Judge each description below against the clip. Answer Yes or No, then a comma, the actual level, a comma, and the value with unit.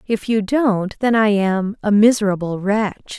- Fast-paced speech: No, average, 150 wpm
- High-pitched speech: Yes, high, 210 Hz